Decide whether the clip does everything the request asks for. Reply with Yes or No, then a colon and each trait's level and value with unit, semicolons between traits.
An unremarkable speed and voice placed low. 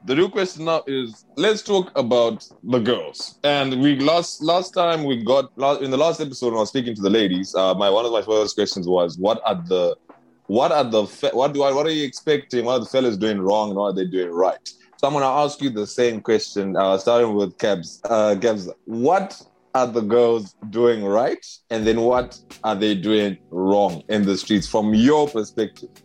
No: fast, 220 wpm; low, 120 Hz